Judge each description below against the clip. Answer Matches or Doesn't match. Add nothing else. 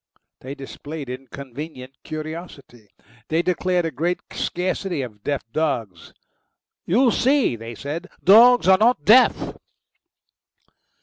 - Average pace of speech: Doesn't match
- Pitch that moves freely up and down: Matches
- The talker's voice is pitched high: Doesn't match